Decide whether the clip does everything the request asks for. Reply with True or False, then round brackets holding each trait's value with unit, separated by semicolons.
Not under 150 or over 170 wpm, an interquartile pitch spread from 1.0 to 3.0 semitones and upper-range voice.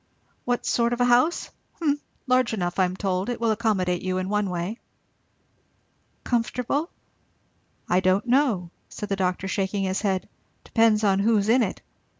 False (160 wpm; 4.3 semitones; 210 Hz)